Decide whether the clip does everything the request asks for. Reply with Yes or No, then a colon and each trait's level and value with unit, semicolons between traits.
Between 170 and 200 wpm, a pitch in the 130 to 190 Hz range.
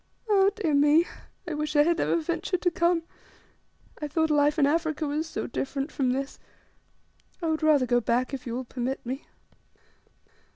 No: average, 175 wpm; very high, 300 Hz